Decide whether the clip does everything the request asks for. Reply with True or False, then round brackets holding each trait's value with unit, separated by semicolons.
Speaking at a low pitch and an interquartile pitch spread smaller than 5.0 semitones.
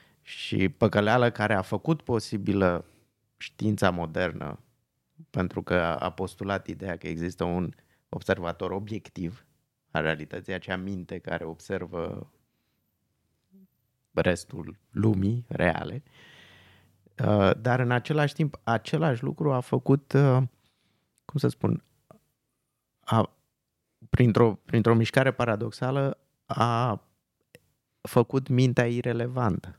False (110 Hz; 5.3 semitones)